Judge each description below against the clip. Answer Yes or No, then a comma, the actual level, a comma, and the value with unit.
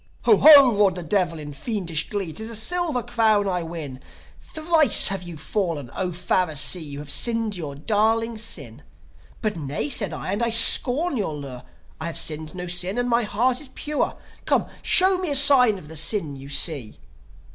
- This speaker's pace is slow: No, average, 190 wpm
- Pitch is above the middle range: Yes, high, 195 Hz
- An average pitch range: No, wide, 6.8 semitones